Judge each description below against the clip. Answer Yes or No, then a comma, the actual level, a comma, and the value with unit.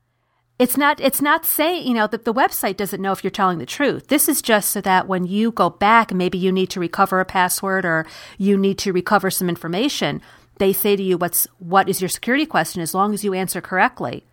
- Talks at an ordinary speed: No, fast, 235 wpm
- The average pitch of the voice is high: Yes, high, 195 Hz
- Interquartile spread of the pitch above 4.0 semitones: No, average, 3.7 semitones